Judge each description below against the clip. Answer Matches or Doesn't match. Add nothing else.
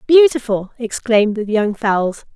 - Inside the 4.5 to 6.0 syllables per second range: Doesn't match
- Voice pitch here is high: Matches